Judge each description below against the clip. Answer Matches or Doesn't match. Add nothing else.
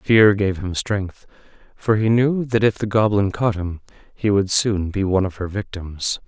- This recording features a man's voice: Matches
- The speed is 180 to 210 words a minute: Matches